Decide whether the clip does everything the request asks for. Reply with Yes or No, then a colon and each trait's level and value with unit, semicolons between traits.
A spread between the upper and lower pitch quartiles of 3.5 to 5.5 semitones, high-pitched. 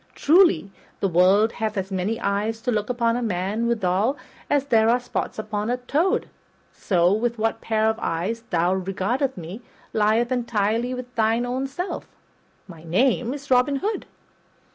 Yes: average, 3.8 semitones; high, 225 Hz